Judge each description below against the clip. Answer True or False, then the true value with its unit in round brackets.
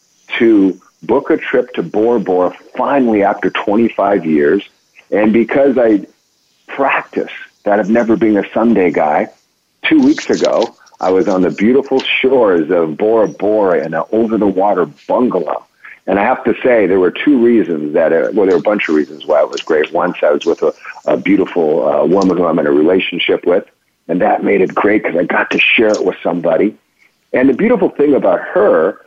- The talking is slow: False (200 wpm)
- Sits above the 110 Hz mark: True (135 Hz)